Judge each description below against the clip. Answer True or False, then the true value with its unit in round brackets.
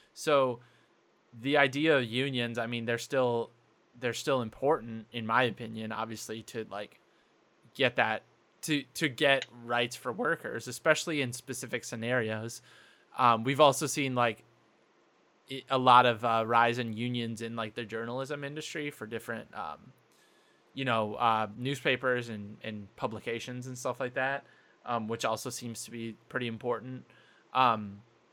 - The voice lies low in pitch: True (120 Hz)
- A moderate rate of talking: True (150 wpm)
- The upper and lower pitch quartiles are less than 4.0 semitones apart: True (2.5 semitones)